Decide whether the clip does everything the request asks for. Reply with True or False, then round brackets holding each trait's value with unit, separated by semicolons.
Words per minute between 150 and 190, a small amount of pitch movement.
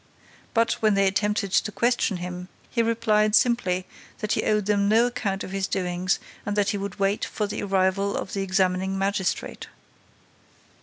True (170 wpm; 1.9 semitones)